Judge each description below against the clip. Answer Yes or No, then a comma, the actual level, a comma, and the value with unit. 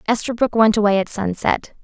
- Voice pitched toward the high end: Yes, high, 215 Hz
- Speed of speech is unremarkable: Yes, average, 165 wpm